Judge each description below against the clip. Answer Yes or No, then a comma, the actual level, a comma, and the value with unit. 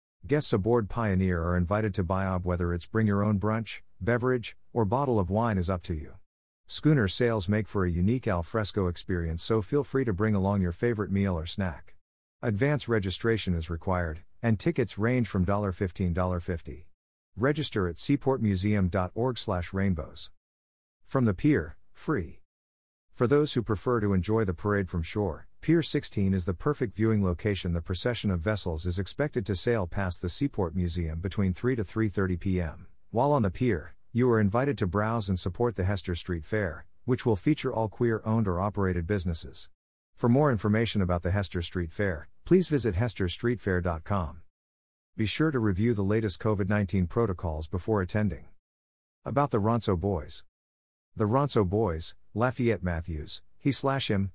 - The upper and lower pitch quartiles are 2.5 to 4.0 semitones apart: No, average, 4.5 semitones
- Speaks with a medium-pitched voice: No, low, 100 Hz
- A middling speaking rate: Yes, average, 165 wpm